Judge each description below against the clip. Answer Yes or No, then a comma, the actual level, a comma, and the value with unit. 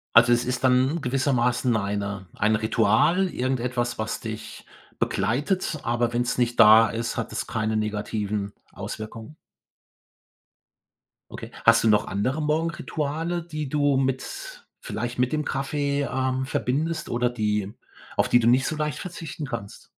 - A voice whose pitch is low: Yes, low, 125 Hz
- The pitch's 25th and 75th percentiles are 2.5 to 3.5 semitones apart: No, average, 4.4 semitones